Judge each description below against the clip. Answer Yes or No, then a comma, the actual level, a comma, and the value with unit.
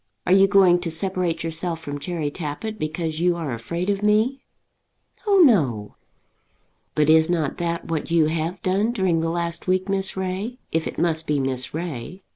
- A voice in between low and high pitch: Yes, medium, 170 Hz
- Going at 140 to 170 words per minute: No, average, 180 wpm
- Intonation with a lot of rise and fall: No, average, 3.1 semitones